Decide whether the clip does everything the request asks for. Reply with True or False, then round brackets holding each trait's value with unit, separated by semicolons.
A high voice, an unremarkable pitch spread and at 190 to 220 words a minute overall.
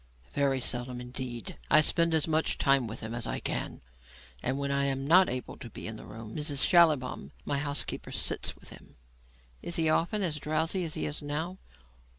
False (140 Hz; 4.1 semitones; 195 wpm)